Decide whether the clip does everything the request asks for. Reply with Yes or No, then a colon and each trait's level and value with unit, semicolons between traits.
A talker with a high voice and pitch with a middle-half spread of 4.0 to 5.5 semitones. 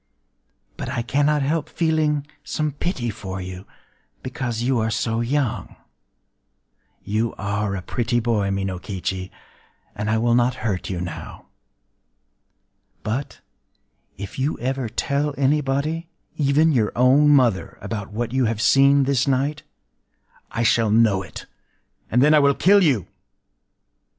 No: low, 120 Hz; average, 4.9 semitones